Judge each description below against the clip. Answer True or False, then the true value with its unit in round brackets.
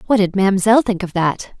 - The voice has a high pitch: True (200 Hz)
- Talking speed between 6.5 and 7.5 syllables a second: False (5.7 syllables/s)